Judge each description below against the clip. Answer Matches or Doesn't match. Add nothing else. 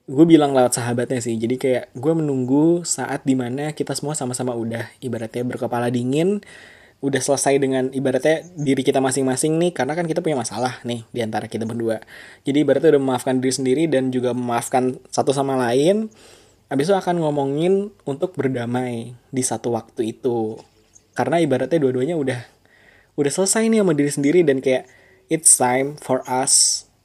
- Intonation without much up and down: Doesn't match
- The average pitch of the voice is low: Matches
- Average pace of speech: Doesn't match